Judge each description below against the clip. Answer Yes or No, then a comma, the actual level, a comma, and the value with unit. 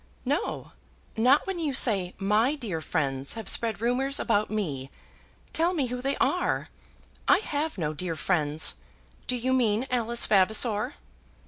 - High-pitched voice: Yes, high, 225 Hz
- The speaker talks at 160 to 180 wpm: No, average, 145 wpm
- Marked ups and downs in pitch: Yes, wide, 6.0 semitones